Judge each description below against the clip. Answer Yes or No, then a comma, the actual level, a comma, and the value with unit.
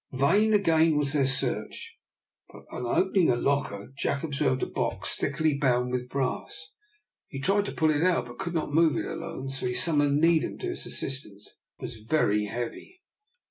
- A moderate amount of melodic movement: Yes, average, 4.5 semitones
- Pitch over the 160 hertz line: No, medium, 140 Hz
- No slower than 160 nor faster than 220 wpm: Yes, average, 180 wpm